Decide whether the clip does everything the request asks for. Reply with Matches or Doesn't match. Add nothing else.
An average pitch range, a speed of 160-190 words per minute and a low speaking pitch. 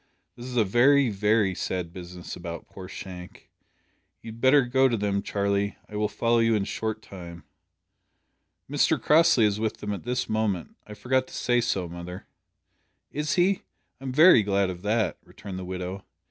Matches